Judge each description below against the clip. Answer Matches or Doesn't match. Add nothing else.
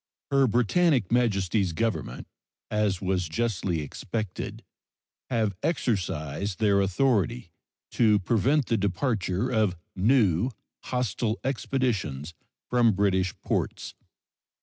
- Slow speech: Matches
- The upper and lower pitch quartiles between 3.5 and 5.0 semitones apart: Matches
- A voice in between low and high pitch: Doesn't match